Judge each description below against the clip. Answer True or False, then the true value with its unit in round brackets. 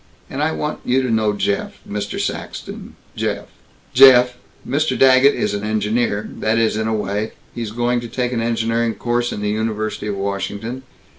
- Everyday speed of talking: True (170 wpm)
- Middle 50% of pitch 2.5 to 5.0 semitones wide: True (2.8 semitones)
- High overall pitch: False (115 Hz)